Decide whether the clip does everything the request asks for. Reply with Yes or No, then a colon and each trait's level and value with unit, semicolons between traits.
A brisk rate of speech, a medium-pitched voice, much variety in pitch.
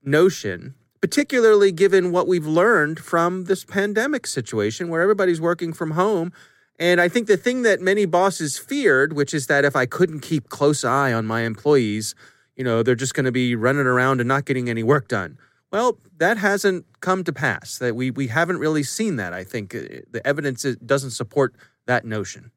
No: average, 190 wpm; medium, 145 Hz; wide, 6.2 semitones